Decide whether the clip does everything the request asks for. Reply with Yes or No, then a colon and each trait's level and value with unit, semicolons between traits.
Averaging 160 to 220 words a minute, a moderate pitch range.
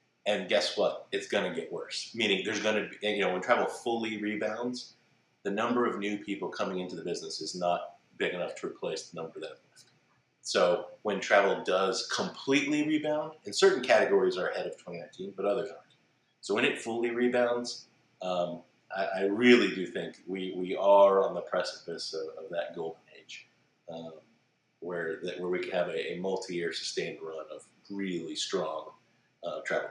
No: average, 185 wpm; wide, 7.2 semitones